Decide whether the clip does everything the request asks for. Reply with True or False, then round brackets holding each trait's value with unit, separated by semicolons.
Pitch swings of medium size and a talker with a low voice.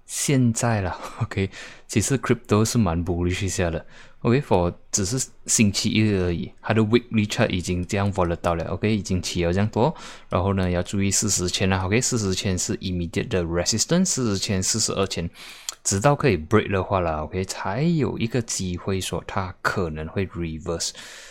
True (3.8 semitones; 100 Hz)